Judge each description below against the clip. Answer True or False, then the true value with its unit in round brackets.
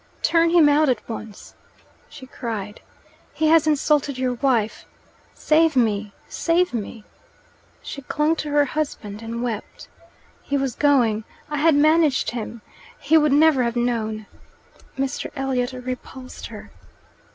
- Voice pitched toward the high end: True (270 Hz)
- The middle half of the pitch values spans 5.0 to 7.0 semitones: False (4.4 semitones)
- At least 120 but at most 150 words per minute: True (140 wpm)